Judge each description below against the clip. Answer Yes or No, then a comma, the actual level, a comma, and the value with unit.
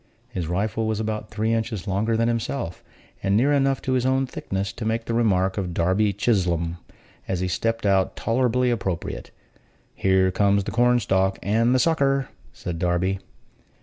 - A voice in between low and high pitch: No, low, 105 Hz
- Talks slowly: No, average, 165 wpm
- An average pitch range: Yes, average, 3.8 semitones